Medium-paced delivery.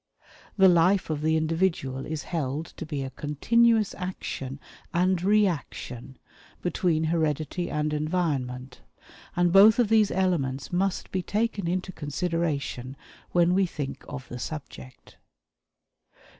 No: slow, 125 wpm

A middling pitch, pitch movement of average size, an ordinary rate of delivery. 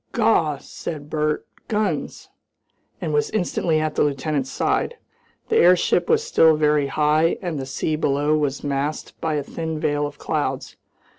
No: medium, 155 Hz; narrow, 2.2 semitones; average, 155 wpm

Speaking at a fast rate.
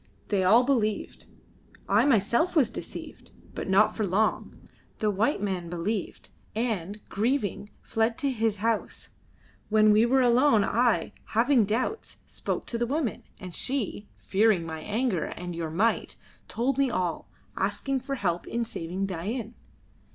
No: average, 145 wpm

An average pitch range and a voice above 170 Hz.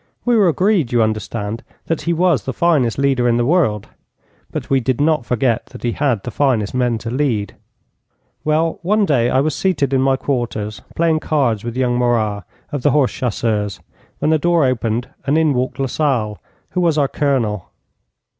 No: average, 4.8 semitones; low, 130 Hz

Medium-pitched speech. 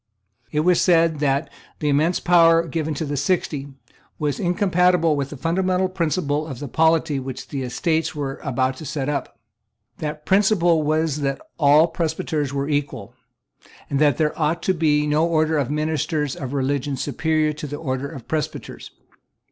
Yes: medium, 150 Hz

